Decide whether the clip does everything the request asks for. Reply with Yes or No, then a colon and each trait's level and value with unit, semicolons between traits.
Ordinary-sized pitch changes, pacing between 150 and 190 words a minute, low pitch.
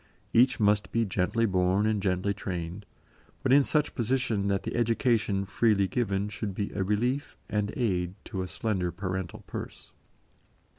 Yes: average, 3.4 semitones; average, 155 wpm; low, 100 Hz